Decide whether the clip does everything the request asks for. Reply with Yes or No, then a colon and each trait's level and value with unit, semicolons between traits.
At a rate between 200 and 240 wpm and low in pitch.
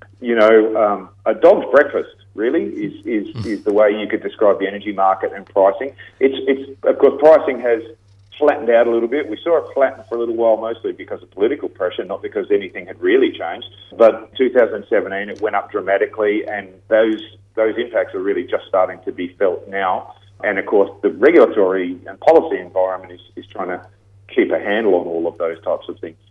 Yes: fast, 205 wpm; low, 115 Hz